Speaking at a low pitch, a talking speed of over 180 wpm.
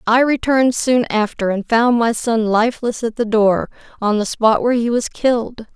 No: high, 230 Hz; average, 200 wpm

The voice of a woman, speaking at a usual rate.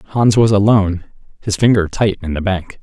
No: male; average, 190 wpm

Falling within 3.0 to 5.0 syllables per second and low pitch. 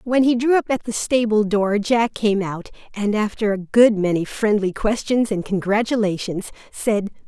No: 4.7 syllables/s; high, 215 Hz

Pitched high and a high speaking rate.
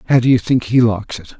No: low, 115 Hz; fast, 300 wpm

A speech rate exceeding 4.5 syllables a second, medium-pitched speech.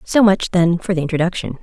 Yes: 6.0 syllables/s; medium, 180 Hz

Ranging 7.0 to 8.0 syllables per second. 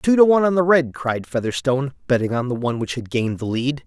No: 6.5 syllables/s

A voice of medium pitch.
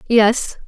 No: high, 225 Hz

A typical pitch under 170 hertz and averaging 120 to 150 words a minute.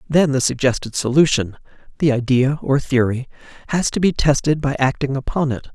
Yes: low, 135 Hz; average, 145 wpm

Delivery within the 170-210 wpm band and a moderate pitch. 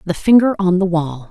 No: fast, 230 wpm; medium, 180 Hz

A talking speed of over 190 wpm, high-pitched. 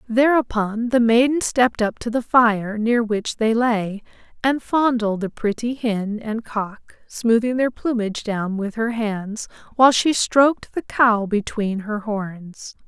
No: average, 160 wpm; high, 225 Hz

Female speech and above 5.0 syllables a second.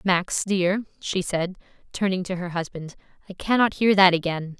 No: female; 4.8 syllables/s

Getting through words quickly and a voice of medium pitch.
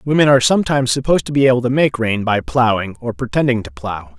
No: fast, 230 wpm; low, 125 Hz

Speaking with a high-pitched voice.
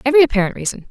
Yes: very high, 250 Hz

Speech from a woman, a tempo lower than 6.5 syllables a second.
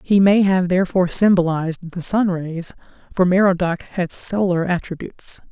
Yes: female; 5.1 syllables/s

